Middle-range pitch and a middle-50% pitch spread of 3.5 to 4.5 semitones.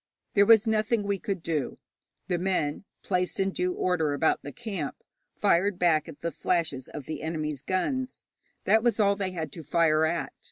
Yes: medium, 180 Hz; average, 4.2 semitones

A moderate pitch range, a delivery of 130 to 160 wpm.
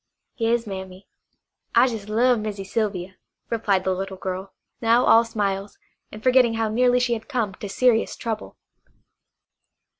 Yes: average, 3.3 semitones; average, 145 wpm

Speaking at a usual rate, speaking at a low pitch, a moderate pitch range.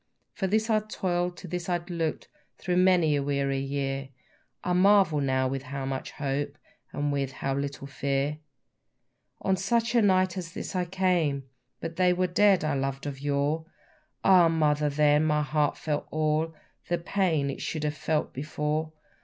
No: average, 170 wpm; medium, 155 Hz; average, 4.2 semitones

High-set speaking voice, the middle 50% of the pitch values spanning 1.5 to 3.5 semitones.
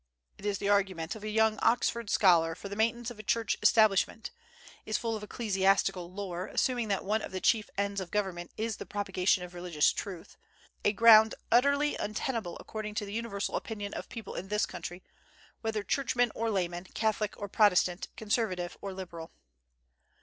Yes: high, 205 Hz; average, 2.9 semitones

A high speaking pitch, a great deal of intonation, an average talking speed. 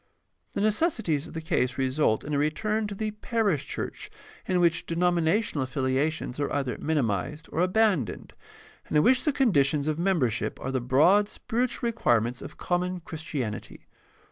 No: medium, 160 Hz; wide, 7.0 semitones; average, 155 wpm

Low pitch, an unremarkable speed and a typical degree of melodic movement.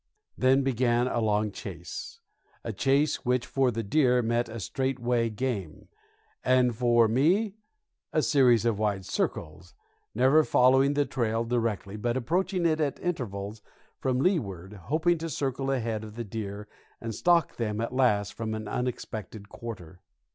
Yes: low, 120 Hz; average, 150 wpm; average, 3.7 semitones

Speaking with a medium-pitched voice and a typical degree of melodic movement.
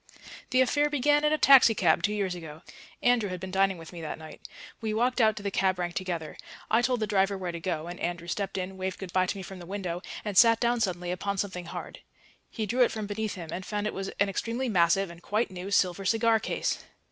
No: high, 195 Hz; average, 3.7 semitones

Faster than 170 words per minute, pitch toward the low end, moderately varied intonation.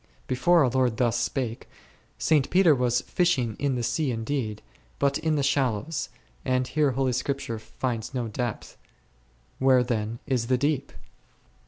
No: average, 150 wpm; low, 130 Hz; average, 3.0 semitones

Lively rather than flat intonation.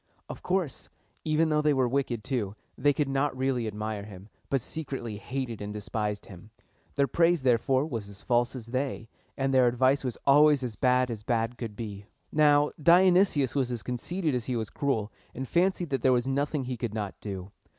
No: average, 4.2 semitones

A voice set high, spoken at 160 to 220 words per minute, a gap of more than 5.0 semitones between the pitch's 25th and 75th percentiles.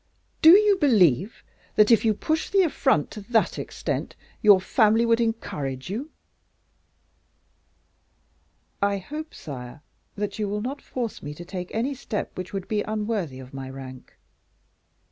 No: high, 210 Hz; average, 145 wpm; wide, 5.5 semitones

